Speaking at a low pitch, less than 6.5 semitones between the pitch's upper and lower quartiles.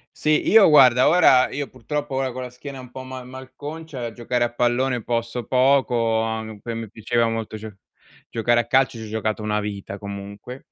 Yes: low, 120 Hz; average, 2.8 semitones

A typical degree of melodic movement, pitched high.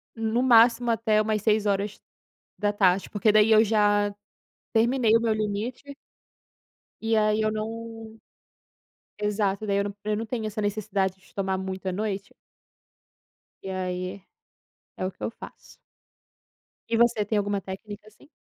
No: narrow, 1.9 semitones; high, 215 Hz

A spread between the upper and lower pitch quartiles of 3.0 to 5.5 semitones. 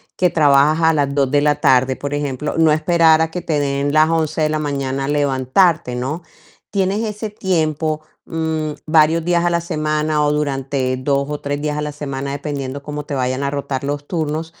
No: narrow, 2.4 semitones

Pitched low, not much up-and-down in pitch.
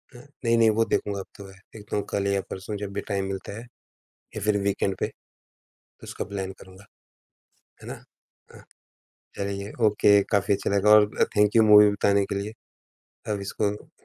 Yes: low, 100 Hz; narrow, 1.0 semitones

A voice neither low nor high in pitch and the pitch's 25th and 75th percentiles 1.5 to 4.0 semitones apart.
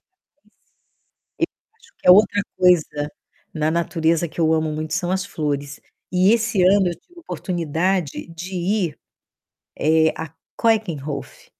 Yes: medium, 170 Hz; average, 3.4 semitones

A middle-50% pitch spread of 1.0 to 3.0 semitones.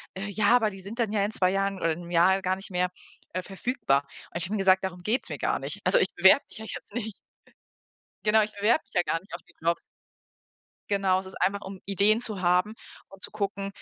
Yes: narrow, 2.4 semitones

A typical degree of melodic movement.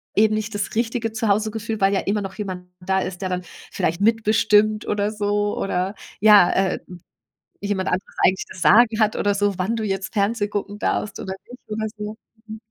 No: narrow, 2.0 semitones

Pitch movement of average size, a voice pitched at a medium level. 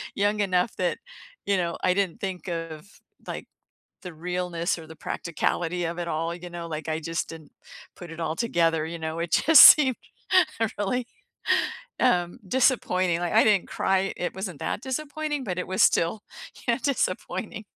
Yes: average, 3.6 semitones; medium, 180 Hz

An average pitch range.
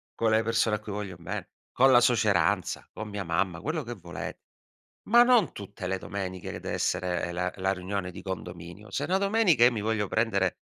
Yes: average, 4.0 semitones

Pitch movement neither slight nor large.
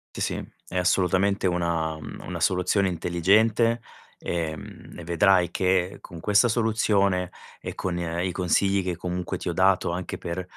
No: narrow, 2.2 semitones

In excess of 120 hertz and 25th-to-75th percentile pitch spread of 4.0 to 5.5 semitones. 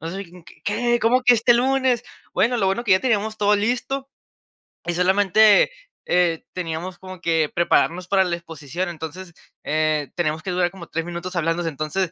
Yes: medium, 185 Hz; average, 4.4 semitones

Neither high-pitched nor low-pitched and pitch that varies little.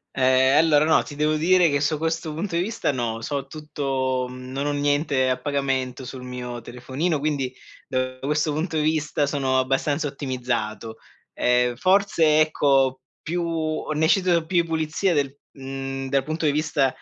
No: medium, 145 Hz; average, 3.1 semitones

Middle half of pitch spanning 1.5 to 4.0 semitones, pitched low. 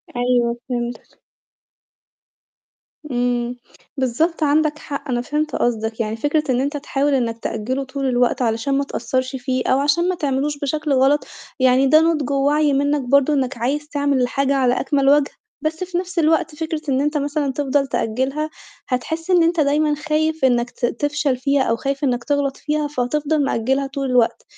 No: average, 3.0 semitones; very high, 275 Hz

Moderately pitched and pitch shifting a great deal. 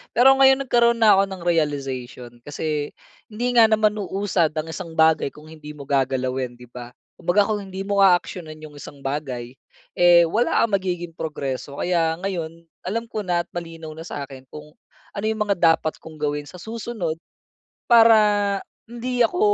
Yes: medium, 170 Hz; wide, 5.9 semitones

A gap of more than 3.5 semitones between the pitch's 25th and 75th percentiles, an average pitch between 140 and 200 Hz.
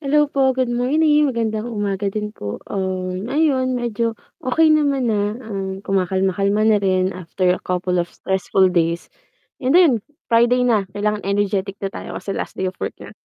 No: average, 4.8 semitones; high, 210 Hz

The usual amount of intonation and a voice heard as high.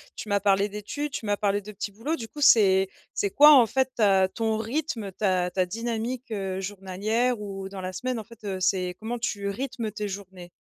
Yes: average, 3.3 semitones; high, 205 Hz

